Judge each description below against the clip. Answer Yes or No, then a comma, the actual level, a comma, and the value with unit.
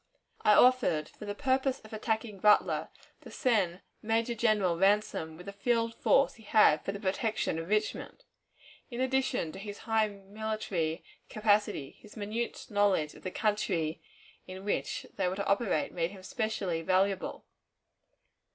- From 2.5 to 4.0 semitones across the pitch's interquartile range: Yes, average, 3.1 semitones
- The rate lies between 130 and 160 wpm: Yes, average, 150 wpm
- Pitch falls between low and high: No, high, 205 Hz